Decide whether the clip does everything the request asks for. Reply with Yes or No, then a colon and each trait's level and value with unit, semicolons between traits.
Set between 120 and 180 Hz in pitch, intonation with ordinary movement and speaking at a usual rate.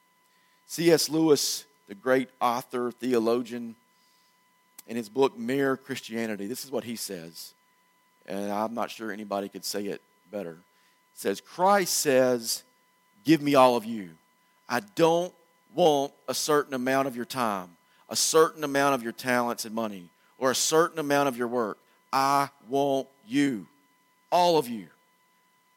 No: low, 135 Hz; wide, 6.0 semitones; average, 150 wpm